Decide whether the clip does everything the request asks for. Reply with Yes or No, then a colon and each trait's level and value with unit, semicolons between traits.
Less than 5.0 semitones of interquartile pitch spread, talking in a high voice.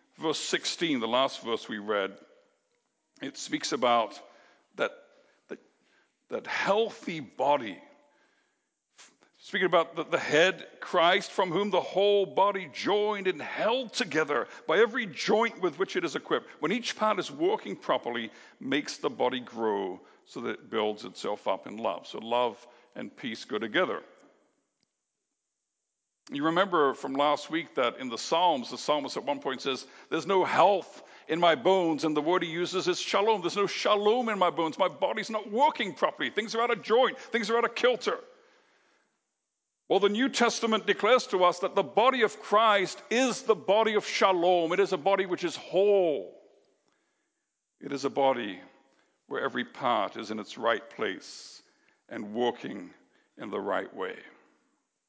No: wide, 5.4 semitones; high, 200 Hz